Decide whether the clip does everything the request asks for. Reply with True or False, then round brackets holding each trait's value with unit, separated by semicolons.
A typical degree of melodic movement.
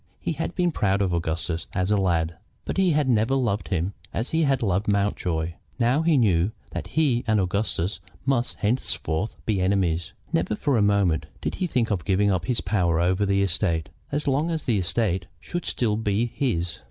False (5.8 semitones)